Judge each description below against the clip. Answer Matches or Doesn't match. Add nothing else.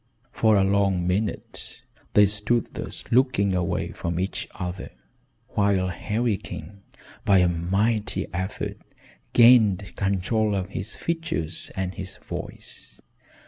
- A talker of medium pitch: Doesn't match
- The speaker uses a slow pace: Matches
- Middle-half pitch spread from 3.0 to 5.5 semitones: Doesn't match